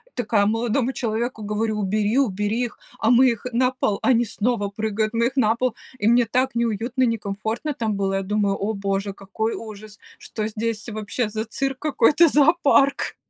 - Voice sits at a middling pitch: No, high, 225 Hz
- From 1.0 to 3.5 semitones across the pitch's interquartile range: Yes, average, 2.9 semitones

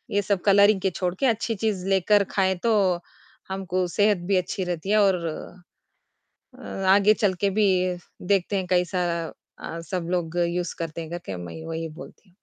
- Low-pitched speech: No, medium, 185 Hz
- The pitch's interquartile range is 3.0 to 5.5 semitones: No, narrow, 2.4 semitones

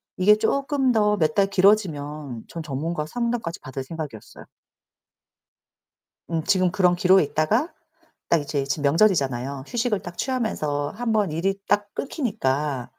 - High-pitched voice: No, medium, 175 Hz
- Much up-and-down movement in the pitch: Yes, wide, 6.4 semitones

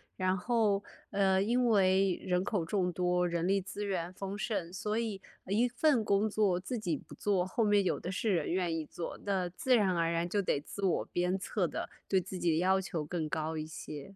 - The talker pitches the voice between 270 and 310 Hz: No, high, 190 Hz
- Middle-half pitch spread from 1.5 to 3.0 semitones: Yes, narrow, 2.6 semitones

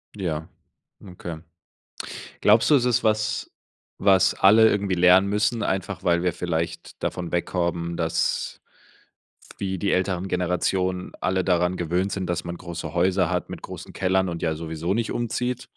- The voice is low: Yes, very low, 90 Hz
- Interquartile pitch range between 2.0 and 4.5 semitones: Yes, narrow, 2.4 semitones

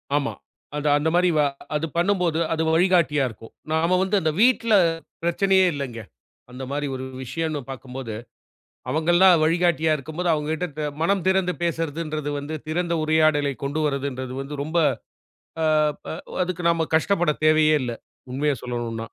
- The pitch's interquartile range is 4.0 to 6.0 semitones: No, average, 3.4 semitones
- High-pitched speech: No, medium, 155 Hz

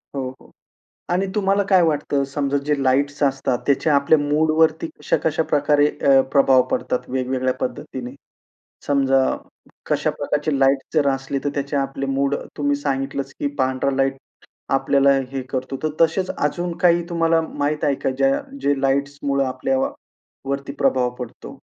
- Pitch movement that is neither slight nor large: No, narrow, 2.1 semitones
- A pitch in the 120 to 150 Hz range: Yes, medium, 140 Hz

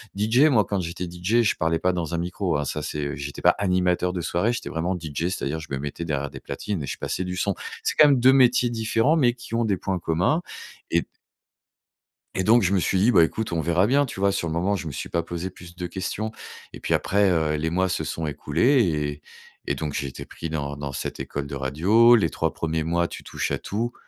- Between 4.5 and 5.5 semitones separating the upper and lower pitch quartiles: Yes, average, 5.1 semitones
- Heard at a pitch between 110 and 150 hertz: No, very low, 90 Hz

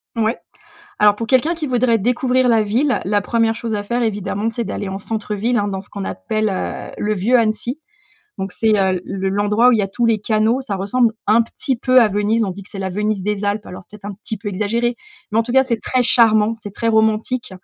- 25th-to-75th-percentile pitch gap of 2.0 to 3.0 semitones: Yes, narrow, 2.6 semitones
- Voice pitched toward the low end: No, high, 215 Hz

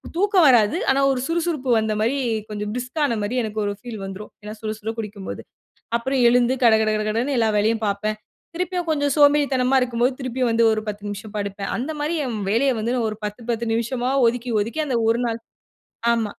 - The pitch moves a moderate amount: Yes, average, 3.6 semitones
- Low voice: No, high, 235 Hz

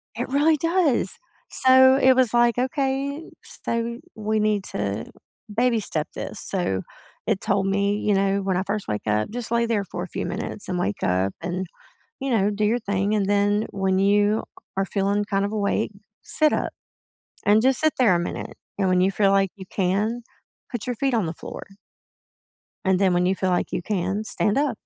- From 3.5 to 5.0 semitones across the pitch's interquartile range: Yes, average, 3.9 semitones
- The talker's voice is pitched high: Yes, high, 205 Hz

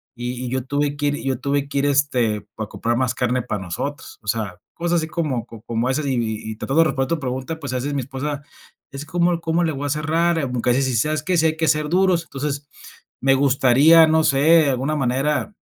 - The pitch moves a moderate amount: Yes, average, 3.7 semitones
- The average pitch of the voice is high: No, medium, 140 Hz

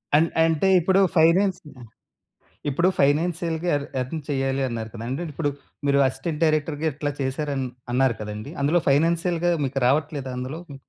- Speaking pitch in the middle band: Yes, medium, 145 Hz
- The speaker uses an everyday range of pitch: Yes, average, 3.6 semitones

